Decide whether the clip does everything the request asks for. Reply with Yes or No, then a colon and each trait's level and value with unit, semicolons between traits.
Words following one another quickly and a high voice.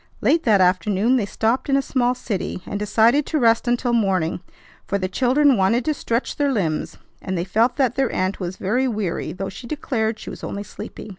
Yes: fast, 210 wpm; high, 225 Hz